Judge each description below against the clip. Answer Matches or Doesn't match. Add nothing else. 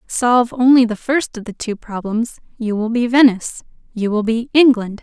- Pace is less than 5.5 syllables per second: Matches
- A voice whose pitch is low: Doesn't match